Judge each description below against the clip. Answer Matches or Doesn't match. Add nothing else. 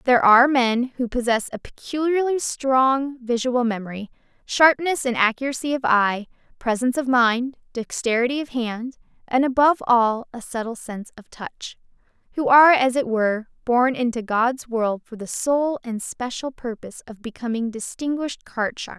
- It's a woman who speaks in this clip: Matches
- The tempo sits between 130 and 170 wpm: Matches